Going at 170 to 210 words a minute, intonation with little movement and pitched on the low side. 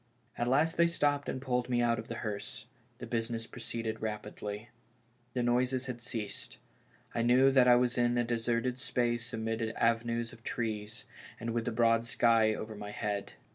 Yes: average, 180 wpm; narrow, 1.6 semitones; low, 120 Hz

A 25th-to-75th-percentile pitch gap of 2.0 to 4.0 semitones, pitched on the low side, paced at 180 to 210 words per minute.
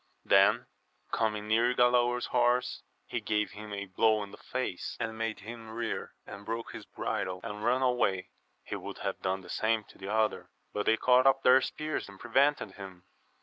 Yes: average, 3.1 semitones; low, 110 Hz; average, 190 wpm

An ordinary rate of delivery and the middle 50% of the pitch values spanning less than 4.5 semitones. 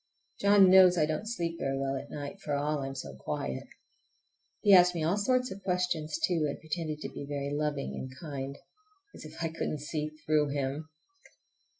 Yes: average, 190 wpm; average, 4.1 semitones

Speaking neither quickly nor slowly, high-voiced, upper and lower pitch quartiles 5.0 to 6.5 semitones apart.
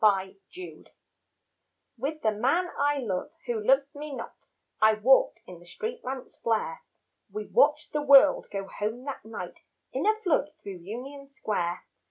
Yes: average, 160 wpm; very high, 250 Hz; wide, 5.6 semitones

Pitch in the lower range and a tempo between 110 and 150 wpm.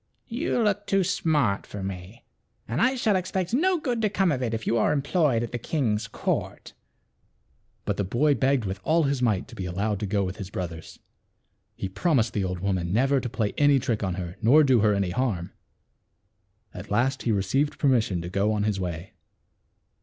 No: low, 115 Hz; average, 200 wpm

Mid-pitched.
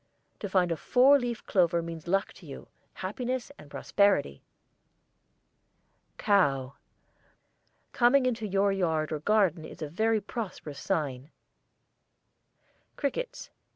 No: high, 195 Hz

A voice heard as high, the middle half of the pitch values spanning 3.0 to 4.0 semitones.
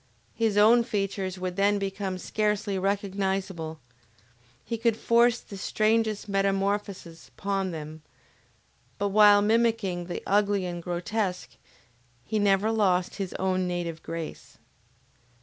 No: high, 195 Hz; narrow, 2.4 semitones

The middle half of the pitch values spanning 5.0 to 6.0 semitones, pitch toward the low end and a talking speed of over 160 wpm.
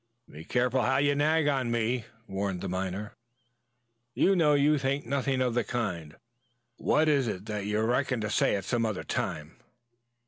Yes: wide, 5.5 semitones; low, 120 Hz; average, 175 wpm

